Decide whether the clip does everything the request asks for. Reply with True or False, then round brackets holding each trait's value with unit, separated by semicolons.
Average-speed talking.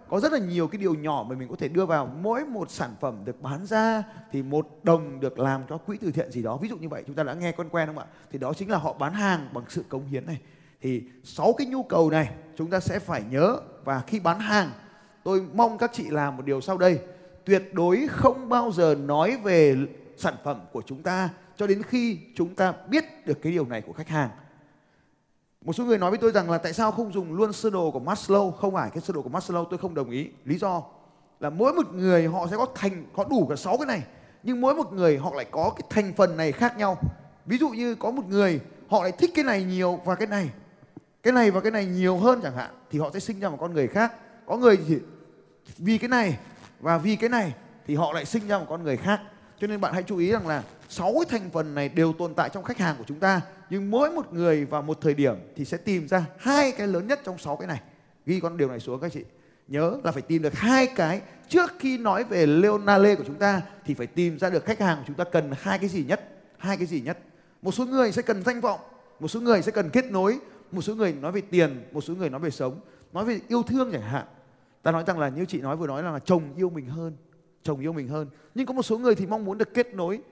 False (265 wpm)